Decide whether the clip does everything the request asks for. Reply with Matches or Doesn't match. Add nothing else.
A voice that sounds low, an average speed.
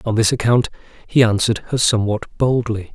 Matches